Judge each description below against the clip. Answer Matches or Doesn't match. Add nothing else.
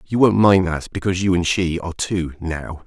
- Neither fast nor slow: Doesn't match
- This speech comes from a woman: Doesn't match